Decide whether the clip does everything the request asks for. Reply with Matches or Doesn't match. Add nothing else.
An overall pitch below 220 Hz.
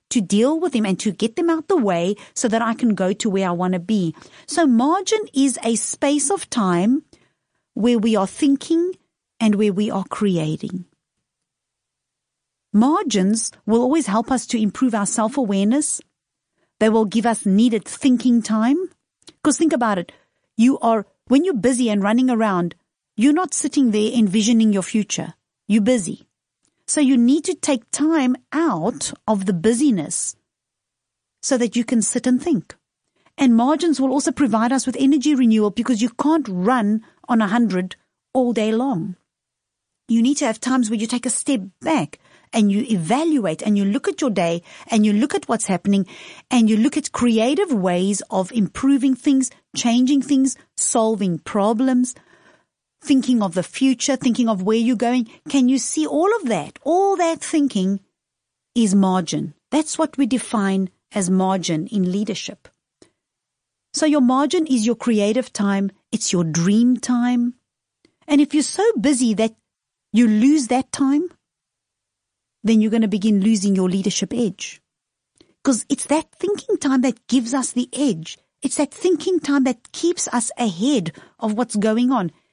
Doesn't match